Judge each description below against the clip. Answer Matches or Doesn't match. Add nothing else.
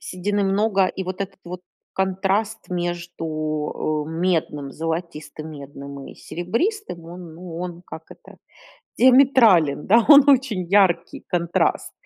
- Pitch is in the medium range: Matches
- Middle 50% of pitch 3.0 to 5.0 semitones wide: Matches